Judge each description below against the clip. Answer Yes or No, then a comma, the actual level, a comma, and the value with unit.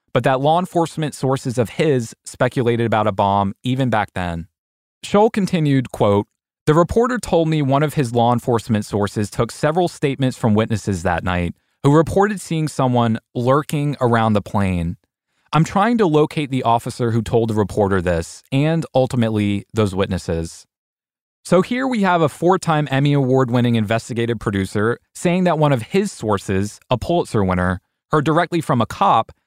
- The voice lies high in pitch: No, low, 125 Hz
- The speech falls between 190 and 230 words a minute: No, average, 165 wpm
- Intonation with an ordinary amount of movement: No, wide, 6.5 semitones